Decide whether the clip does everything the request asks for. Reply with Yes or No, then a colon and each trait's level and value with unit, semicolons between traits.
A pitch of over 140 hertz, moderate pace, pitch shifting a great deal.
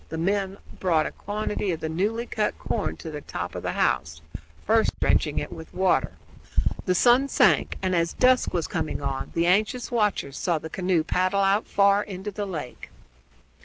No: medium, 185 Hz; average, 190 wpm; average, 4.2 semitones